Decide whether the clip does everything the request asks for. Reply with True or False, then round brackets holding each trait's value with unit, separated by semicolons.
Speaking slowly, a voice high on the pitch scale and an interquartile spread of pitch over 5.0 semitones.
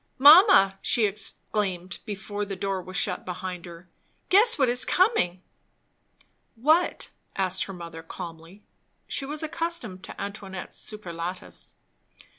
True (120 wpm; 195 Hz; 5.6 semitones)